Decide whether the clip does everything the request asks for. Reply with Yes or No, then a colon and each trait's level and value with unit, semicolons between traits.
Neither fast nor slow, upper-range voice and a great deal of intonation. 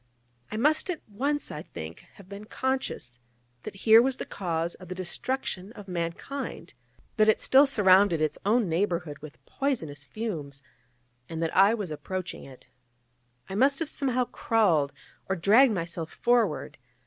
Yes: average, 155 wpm; high, 195 Hz; wide, 6.5 semitones